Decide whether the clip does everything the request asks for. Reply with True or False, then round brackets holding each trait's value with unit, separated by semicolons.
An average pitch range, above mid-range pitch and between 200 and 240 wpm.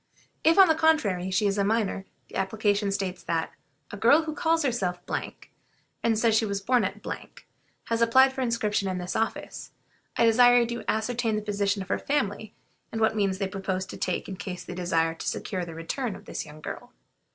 True (3.8 semitones; 210 Hz; 205 wpm)